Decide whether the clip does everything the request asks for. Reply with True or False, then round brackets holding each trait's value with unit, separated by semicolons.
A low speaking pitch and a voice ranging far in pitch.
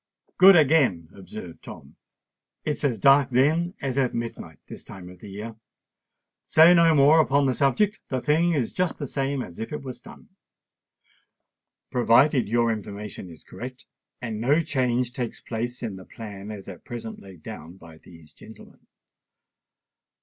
True (120 Hz; 5.8 semitones)